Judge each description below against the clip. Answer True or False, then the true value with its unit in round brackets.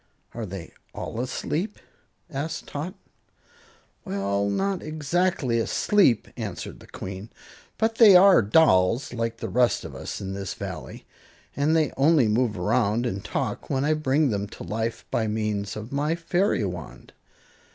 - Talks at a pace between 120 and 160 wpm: True (150 wpm)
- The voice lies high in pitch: False (120 Hz)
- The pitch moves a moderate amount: False (7.1 semitones)